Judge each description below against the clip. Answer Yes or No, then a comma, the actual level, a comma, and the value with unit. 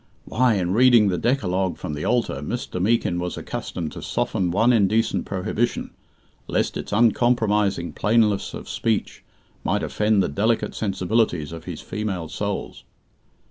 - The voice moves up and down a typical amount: Yes, average, 4.1 semitones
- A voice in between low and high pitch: No, low, 105 Hz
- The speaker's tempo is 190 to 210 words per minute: No, average, 140 wpm